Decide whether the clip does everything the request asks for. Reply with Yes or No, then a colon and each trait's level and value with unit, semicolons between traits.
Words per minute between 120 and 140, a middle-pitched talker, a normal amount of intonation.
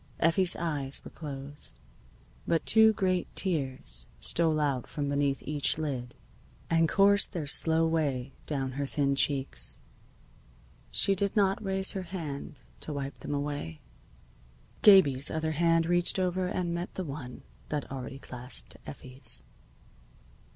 Yes: slow, 135 wpm; medium, 150 Hz; average, 4.3 semitones